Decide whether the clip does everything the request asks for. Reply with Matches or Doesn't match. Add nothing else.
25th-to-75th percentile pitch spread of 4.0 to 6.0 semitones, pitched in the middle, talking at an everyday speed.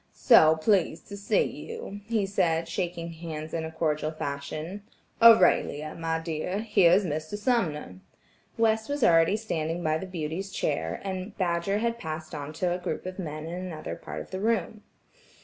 Matches